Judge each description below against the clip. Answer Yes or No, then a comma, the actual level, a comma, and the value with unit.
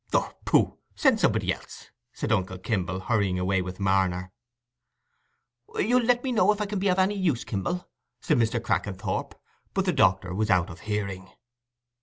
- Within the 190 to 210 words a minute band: No, average, 165 wpm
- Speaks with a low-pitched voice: Yes, low, 100 Hz